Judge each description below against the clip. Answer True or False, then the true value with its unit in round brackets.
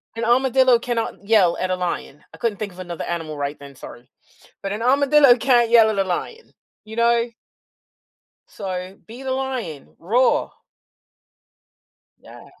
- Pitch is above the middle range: True (220 Hz)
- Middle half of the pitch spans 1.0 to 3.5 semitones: False (5.2 semitones)